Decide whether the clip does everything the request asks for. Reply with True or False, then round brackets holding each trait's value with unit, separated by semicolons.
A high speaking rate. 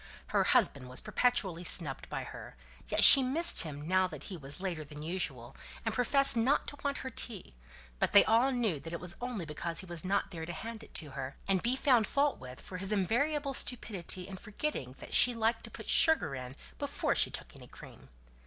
True (215 wpm)